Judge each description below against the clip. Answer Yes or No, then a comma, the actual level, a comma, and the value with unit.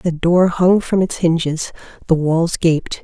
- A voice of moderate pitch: Yes, medium, 170 Hz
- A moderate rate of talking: Yes, average, 180 wpm